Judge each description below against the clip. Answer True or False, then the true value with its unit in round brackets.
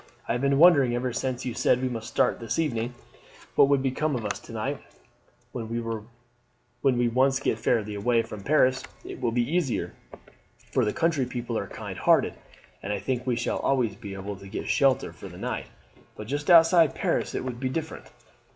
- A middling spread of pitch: True (3.0 semitones)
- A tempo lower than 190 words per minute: False (195 wpm)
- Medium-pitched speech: False (120 Hz)